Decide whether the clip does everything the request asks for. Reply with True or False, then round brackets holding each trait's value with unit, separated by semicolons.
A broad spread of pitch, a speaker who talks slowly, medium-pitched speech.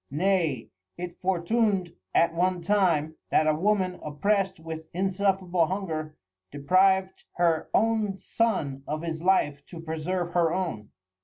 False (3.2 semitones; 130 wpm; 175 Hz)